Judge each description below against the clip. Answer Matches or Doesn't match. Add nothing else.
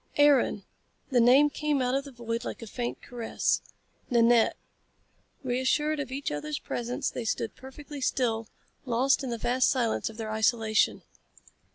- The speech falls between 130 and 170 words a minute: Matches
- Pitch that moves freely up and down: Doesn't match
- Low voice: Doesn't match